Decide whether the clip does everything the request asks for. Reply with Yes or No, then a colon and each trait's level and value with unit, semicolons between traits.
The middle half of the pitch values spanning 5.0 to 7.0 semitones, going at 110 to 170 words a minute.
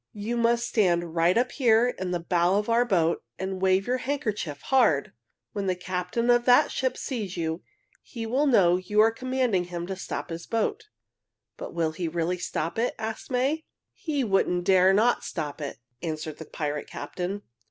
No: wide, 5.6 semitones; average, 185 wpm